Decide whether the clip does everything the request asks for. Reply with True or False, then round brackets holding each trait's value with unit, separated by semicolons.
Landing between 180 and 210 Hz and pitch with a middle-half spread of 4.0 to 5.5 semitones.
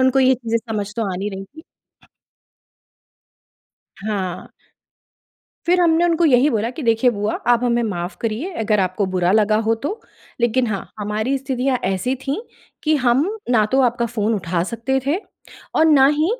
False (235 Hz; 4.3 semitones)